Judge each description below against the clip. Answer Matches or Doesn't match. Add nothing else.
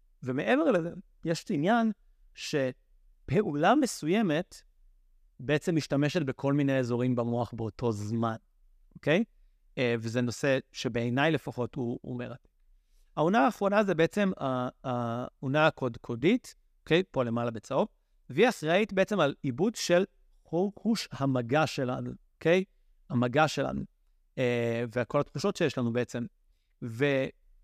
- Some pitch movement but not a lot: Doesn't match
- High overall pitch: Doesn't match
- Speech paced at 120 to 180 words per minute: Doesn't match